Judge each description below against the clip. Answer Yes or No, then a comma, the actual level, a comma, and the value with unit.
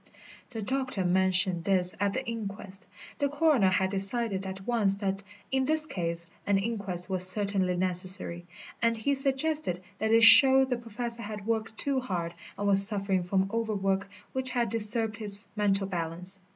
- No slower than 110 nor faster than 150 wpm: No, average, 165 wpm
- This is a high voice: Yes, high, 205 Hz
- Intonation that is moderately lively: Yes, average, 3.5 semitones